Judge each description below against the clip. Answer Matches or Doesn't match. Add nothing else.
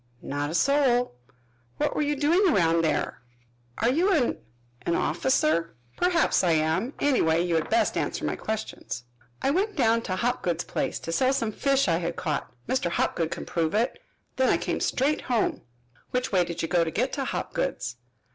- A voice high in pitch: Matches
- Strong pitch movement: Matches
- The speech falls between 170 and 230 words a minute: Matches